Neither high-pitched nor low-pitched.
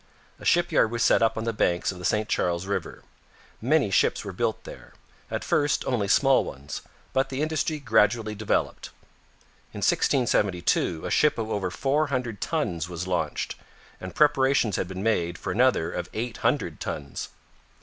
No: low, 110 Hz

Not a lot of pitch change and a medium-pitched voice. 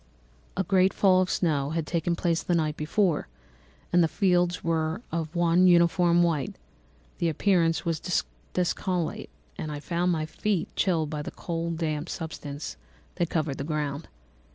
Yes: narrow, 2.3 semitones; medium, 170 Hz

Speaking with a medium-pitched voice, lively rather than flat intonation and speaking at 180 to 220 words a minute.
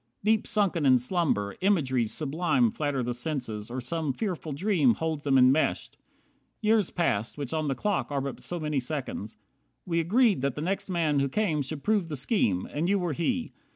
Yes: medium, 155 Hz; wide, 5.8 semitones; average, 190 wpm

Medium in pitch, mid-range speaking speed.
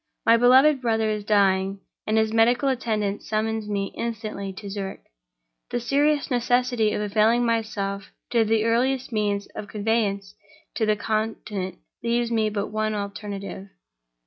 No: high, 215 Hz; average, 145 wpm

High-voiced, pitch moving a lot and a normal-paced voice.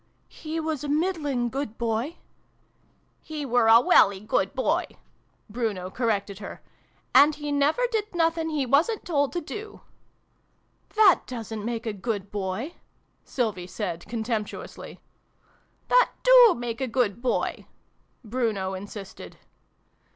Yes: high, 245 Hz; wide, 6.4 semitones; average, 155 wpm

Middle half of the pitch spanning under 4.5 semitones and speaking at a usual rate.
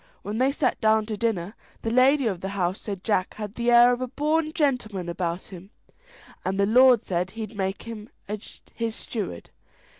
Yes: average, 4.1 semitones; average, 185 wpm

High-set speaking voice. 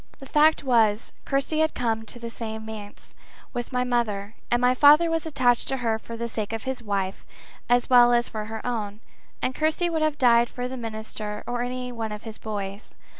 Yes: high, 240 Hz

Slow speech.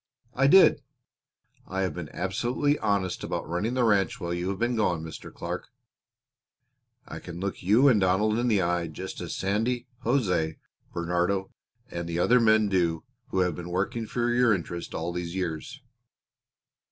No: average, 165 wpm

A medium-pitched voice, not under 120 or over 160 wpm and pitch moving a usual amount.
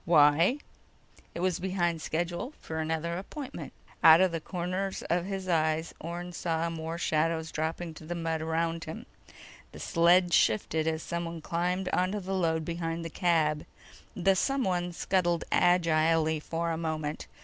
No: medium, 170 Hz; average, 150 wpm; narrow, 1.8 semitones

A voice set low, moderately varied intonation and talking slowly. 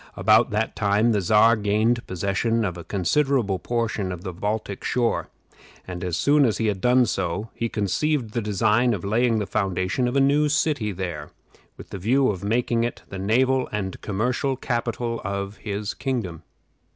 No: low, 110 Hz; average, 3.7 semitones; average, 175 wpm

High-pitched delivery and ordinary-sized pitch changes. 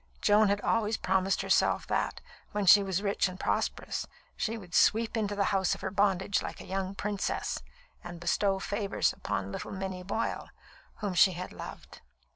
No: high, 195 Hz; narrow, 1.7 semitones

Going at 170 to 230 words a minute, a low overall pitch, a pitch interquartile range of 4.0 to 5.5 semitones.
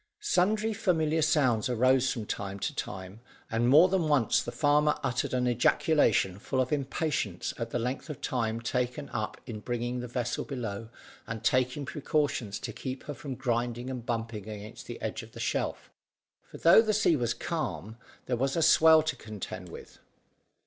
Yes: average, 175 wpm; low, 125 Hz; average, 4.5 semitones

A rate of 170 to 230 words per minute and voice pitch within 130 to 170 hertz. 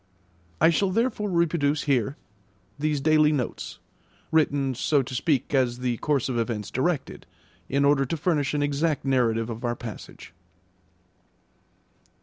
No: slow, 135 wpm; medium, 140 Hz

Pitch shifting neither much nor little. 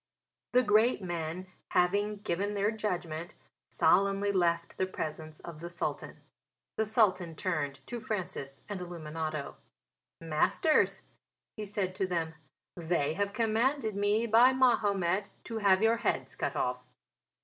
Yes: average, 4.1 semitones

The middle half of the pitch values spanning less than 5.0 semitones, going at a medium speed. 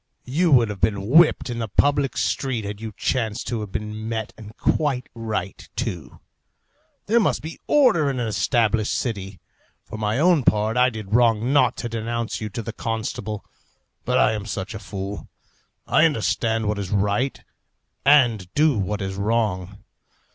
Yes: average, 3.3 semitones; average, 170 wpm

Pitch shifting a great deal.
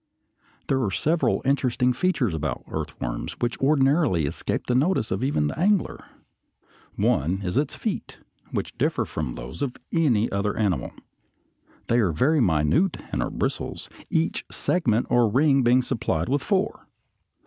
Yes: wide, 7.6 semitones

